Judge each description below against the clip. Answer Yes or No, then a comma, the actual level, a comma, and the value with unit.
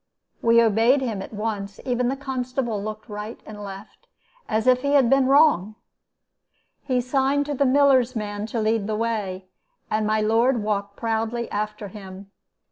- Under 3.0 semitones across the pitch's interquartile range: No, average, 3.4 semitones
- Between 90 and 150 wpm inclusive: No, average, 170 wpm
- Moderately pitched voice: No, high, 225 Hz